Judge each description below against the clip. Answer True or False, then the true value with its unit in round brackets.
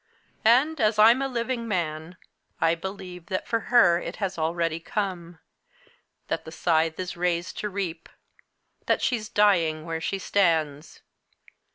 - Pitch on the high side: False (180 Hz)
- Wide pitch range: False (4.3 semitones)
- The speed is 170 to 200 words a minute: False (145 wpm)